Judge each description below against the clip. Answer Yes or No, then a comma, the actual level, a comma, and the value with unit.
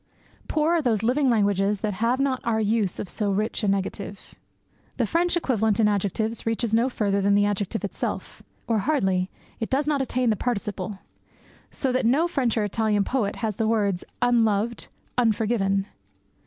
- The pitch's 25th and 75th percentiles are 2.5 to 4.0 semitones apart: Yes, average, 3.4 semitones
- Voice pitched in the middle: No, high, 220 Hz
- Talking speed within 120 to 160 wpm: No, average, 170 wpm